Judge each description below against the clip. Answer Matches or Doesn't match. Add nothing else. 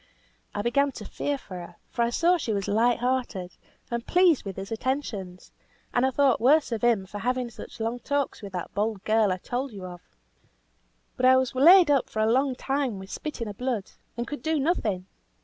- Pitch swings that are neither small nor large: Matches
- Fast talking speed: Matches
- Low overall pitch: Doesn't match